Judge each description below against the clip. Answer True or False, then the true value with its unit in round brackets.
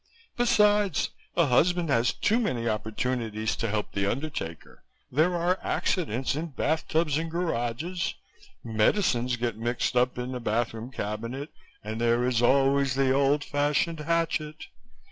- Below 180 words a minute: True (140 wpm)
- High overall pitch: False (135 Hz)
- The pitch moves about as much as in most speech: False (5.7 semitones)